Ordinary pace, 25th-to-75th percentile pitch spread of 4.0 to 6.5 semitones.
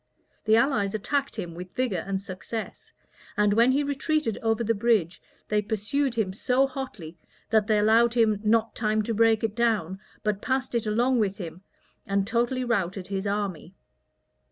No: average, 170 wpm; average, 3.1 semitones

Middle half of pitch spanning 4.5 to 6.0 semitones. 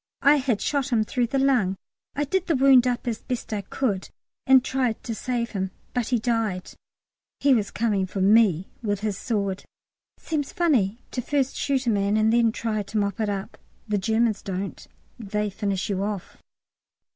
No: average, 4.1 semitones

